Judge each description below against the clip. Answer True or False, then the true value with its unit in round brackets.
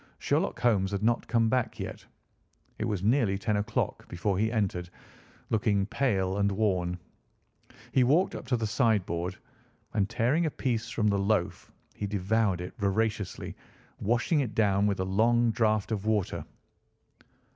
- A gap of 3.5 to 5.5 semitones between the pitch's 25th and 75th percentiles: False (2.9 semitones)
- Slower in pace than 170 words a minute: True (155 wpm)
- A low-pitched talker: True (105 Hz)